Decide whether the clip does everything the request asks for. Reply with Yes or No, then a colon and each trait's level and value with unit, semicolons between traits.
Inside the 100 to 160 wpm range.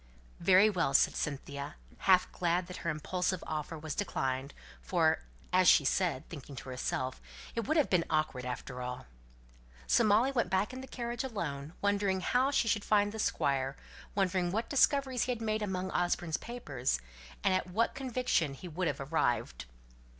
No: average, 170 wpm